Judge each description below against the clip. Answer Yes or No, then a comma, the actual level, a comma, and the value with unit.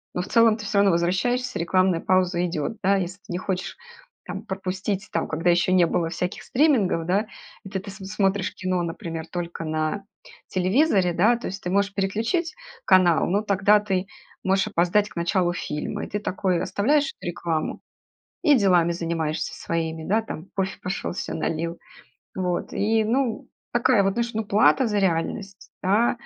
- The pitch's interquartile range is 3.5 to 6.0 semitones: No, average, 3.1 semitones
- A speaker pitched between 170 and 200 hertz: Yes, high, 190 Hz